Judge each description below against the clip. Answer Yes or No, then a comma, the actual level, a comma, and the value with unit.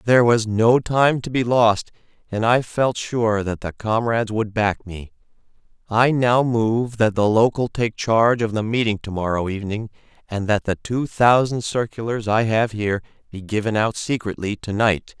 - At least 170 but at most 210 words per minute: Yes, average, 180 wpm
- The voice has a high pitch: No, low, 110 Hz